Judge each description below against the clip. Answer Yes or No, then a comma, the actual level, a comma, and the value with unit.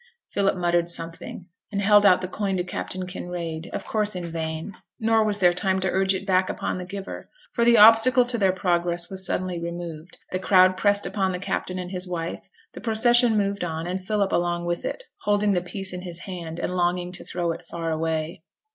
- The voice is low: No, medium, 185 Hz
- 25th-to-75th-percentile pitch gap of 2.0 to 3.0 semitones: Yes, narrow, 2.6 semitones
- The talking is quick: Yes, fast, 210 wpm